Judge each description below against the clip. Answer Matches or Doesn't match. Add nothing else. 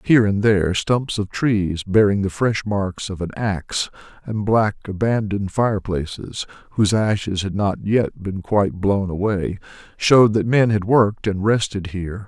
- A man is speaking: Matches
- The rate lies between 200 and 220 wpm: Doesn't match